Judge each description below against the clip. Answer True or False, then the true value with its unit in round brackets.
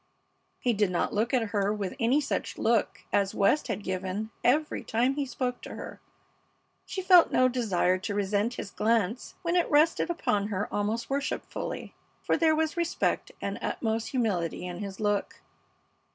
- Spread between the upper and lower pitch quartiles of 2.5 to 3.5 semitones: False (5.0 semitones)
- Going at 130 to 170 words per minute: True (165 wpm)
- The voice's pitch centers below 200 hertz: False (225 Hz)